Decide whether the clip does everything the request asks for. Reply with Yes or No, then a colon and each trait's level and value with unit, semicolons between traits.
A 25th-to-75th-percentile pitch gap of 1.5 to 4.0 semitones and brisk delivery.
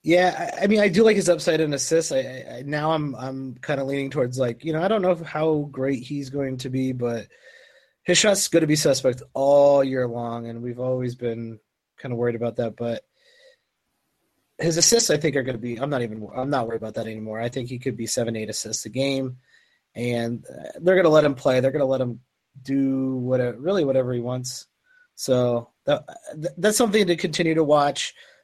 No: average, 4.9 semitones; fast, 215 wpm